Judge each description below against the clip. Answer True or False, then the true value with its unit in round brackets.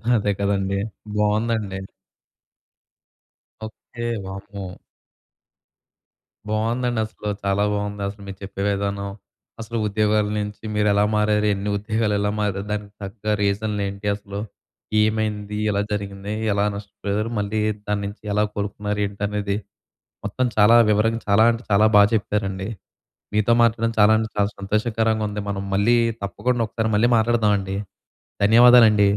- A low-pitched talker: True (105 Hz)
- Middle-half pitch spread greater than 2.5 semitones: False (1.4 semitones)